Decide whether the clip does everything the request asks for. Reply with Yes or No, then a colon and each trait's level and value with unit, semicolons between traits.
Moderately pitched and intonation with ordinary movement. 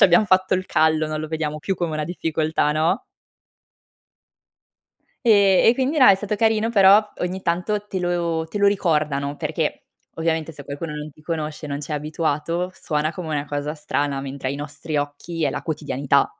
Yes: medium, 160 Hz; average, 3.8 semitones